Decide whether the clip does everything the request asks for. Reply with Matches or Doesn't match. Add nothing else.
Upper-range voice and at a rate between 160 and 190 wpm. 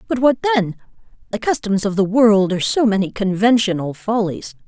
Matches